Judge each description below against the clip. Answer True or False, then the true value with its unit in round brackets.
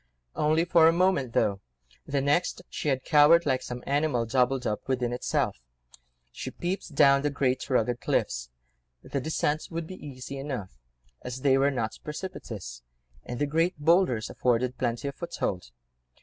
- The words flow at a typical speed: True (155 wpm)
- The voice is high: False (135 Hz)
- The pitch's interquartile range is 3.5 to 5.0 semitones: True (4.1 semitones)